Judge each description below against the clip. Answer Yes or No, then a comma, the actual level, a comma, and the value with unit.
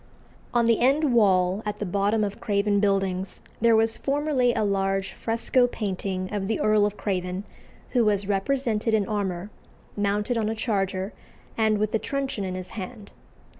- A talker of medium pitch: No, high, 210 Hz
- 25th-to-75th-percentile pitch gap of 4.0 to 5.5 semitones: No, average, 2.8 semitones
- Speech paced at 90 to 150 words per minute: No, average, 170 wpm